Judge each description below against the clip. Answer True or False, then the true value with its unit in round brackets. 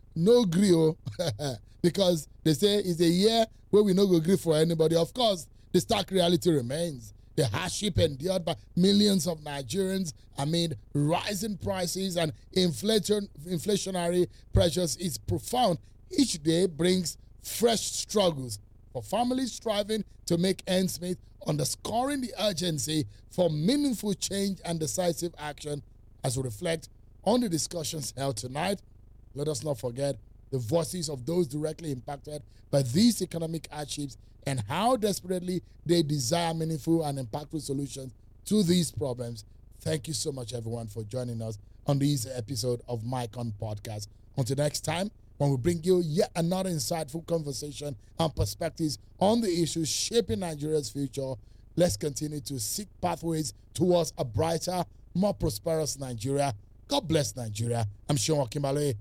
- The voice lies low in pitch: False (155 Hz)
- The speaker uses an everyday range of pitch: False (5.8 semitones)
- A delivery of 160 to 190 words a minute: False (145 wpm)